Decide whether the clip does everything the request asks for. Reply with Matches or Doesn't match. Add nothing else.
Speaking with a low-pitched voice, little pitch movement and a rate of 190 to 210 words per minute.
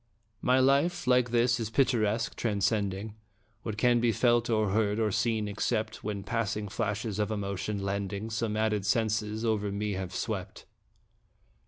Doesn't match